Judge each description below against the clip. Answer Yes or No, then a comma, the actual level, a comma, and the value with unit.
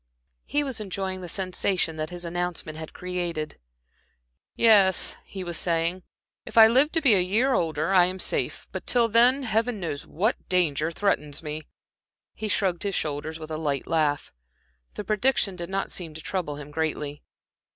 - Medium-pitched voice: Yes, medium, 180 Hz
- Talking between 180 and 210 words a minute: No, average, 170 wpm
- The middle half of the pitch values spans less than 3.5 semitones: No, average, 4.6 semitones